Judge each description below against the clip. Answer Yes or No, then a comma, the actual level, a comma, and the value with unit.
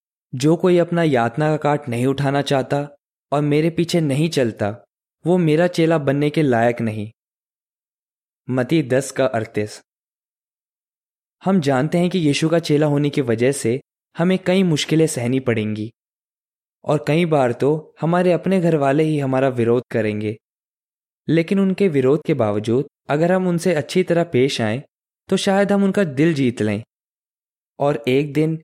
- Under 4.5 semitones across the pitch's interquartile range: No, average, 5.3 semitones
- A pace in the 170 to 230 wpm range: No, average, 155 wpm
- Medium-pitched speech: Yes, medium, 145 Hz